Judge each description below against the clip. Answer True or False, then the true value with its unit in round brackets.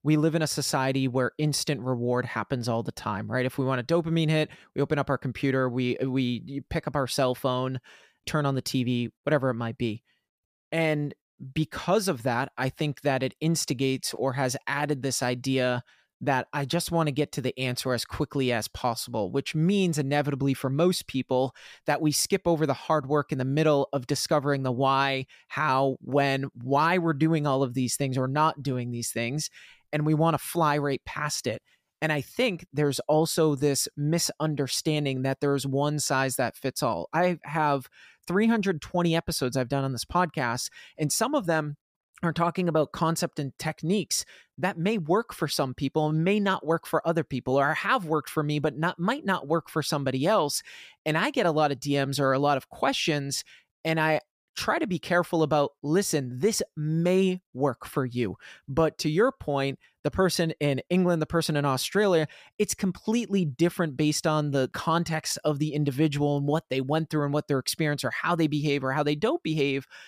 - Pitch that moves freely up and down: False (3.3 semitones)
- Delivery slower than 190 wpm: False (200 wpm)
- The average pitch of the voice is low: False (150 Hz)